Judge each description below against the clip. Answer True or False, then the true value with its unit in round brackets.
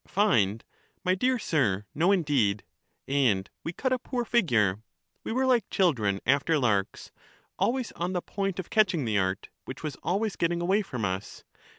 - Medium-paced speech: True (170 wpm)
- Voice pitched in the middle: True (165 Hz)